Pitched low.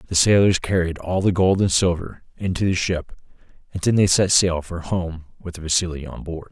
Yes: very low, 90 Hz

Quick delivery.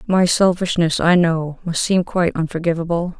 No: average, 150 wpm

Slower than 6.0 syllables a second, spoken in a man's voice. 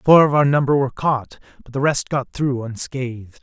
Yes: 5.3 syllables/s; male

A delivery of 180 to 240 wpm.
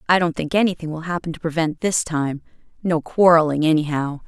No: average, 170 wpm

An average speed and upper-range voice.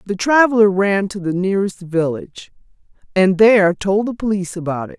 Yes: average, 170 wpm; high, 195 Hz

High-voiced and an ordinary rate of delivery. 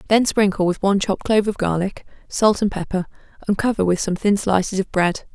No: high, 195 Hz; fast, 215 wpm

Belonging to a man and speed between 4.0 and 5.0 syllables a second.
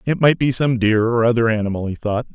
No: male; 6.0 syllables/s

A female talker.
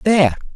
No: male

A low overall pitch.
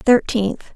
No: high, 220 Hz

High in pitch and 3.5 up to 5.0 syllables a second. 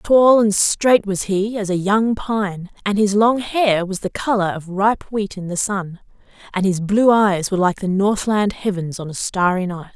Yes: high, 200 Hz; 4.4 syllables/s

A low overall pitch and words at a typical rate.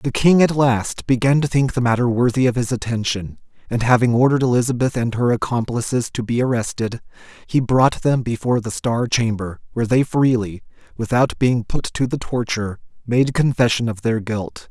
Yes: low, 120 Hz; average, 180 wpm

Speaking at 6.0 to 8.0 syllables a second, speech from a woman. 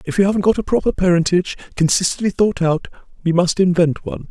No: 6.6 syllables/s; male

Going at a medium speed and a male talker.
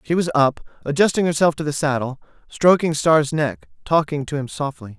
Yes: average, 180 wpm; male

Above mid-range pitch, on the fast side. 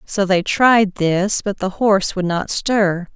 No: high, 195 Hz; average, 190 wpm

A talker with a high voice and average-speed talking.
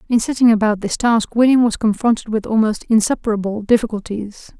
Yes: high, 220 Hz; average, 155 wpm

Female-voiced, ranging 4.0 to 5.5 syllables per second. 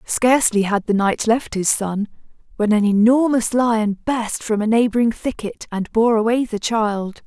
Yes: female; 4.4 syllables/s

